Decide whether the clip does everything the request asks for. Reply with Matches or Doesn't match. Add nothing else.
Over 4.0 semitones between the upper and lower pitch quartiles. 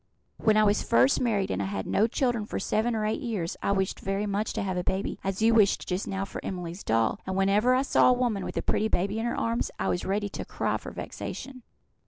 Doesn't match